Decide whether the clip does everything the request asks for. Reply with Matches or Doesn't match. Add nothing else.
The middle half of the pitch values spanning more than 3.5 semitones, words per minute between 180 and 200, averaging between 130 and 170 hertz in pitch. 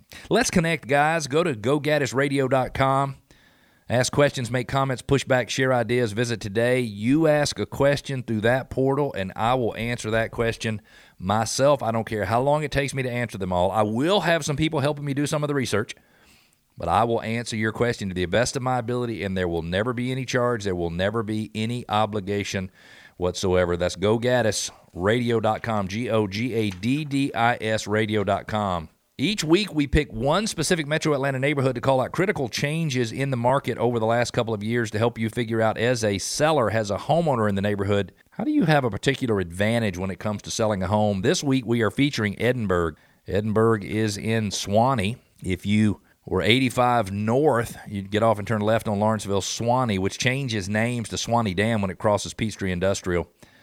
Doesn't match